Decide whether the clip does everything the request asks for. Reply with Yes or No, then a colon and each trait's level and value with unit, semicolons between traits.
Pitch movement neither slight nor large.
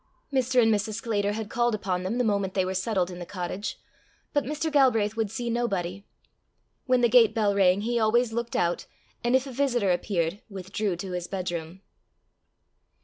Yes: average, 4.2 semitones